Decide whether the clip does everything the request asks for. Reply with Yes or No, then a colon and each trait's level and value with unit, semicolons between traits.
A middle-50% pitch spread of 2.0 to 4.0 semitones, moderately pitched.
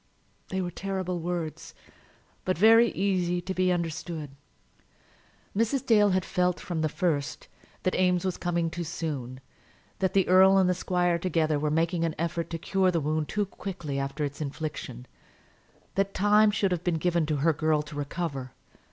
Yes: average, 3.1 semitones; medium, 175 Hz